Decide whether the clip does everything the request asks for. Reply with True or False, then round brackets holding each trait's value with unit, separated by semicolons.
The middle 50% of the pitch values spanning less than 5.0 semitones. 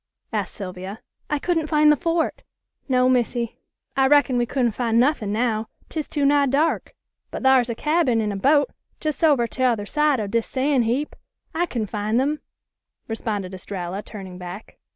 False (5.3 semitones)